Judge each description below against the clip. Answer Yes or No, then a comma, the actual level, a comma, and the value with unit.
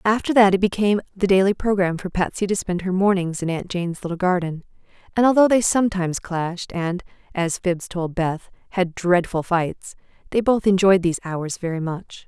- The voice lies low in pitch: No, medium, 185 Hz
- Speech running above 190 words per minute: No, average, 185 wpm